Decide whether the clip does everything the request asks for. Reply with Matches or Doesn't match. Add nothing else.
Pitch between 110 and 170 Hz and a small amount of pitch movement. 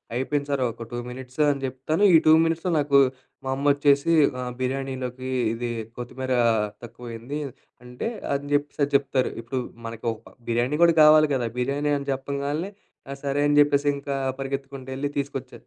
Matches